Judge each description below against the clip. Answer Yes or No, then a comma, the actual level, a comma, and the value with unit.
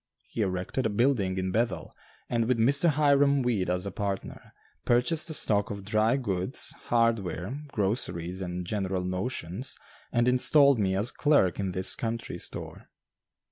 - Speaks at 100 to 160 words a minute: Yes, average, 150 wpm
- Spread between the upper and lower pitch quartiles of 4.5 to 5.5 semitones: Yes, average, 5.1 semitones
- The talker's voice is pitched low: Yes, low, 105 Hz